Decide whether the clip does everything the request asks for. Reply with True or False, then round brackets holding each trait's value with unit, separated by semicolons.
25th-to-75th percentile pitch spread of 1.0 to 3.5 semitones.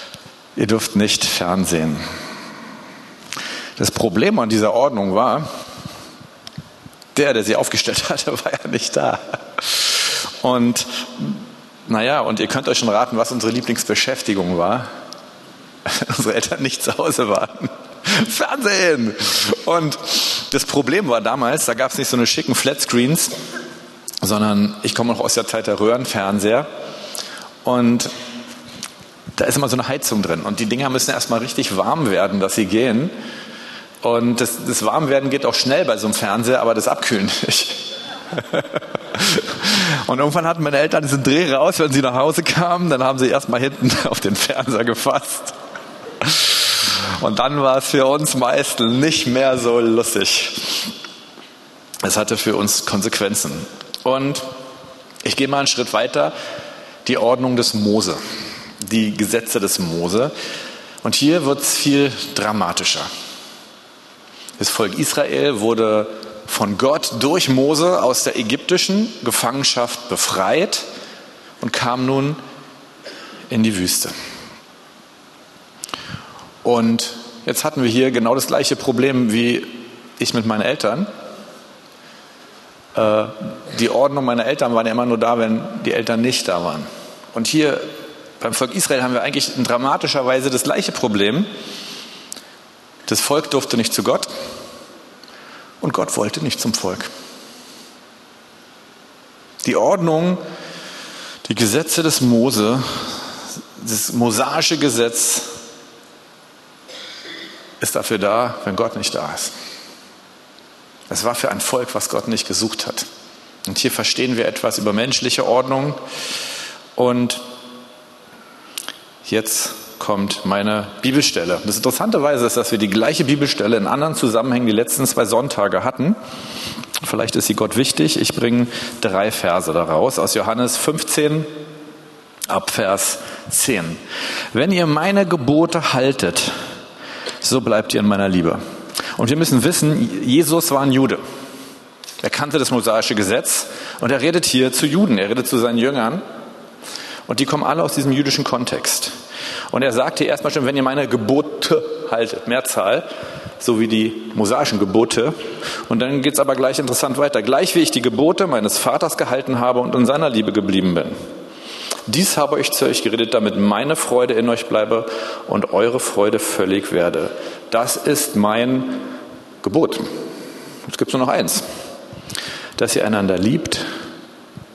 False (3.9 semitones)